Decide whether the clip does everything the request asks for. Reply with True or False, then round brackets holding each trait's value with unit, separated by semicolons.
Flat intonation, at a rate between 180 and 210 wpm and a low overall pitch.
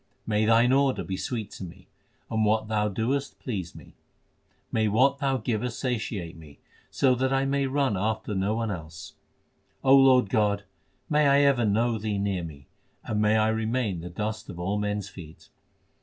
False (4.1 semitones; 185 wpm; 110 Hz)